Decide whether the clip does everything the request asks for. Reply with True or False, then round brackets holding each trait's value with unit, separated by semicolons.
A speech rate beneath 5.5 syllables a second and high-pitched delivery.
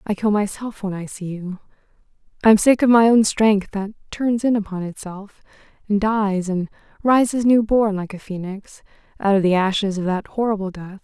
True (5.0 syllables/s; 205 Hz)